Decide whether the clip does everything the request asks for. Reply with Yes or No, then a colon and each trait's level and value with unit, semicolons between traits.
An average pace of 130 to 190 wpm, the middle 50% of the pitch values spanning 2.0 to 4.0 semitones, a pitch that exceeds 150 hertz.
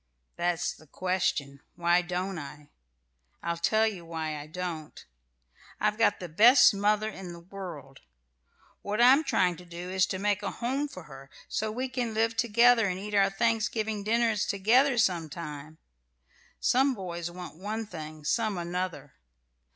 No: average, 160 wpm; average, 4.4 semitones; high, 190 Hz